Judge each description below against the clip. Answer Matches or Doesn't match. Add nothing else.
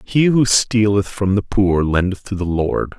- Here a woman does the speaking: Doesn't match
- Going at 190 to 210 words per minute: Matches